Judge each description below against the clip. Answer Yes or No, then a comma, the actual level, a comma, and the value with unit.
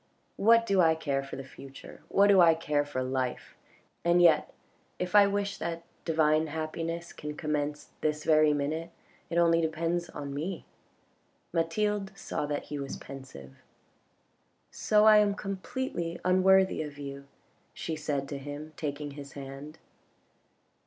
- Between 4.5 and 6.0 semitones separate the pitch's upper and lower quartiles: No, average, 3.6 semitones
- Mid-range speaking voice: Yes, medium, 160 Hz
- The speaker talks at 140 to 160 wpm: Yes, average, 150 wpm